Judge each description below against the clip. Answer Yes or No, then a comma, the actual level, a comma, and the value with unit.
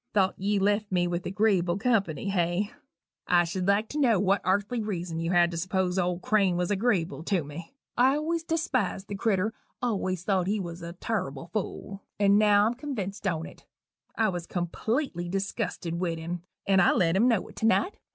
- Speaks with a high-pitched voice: Yes, high, 195 Hz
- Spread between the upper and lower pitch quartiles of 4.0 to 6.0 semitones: No, average, 3.5 semitones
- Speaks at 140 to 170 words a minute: No, average, 185 wpm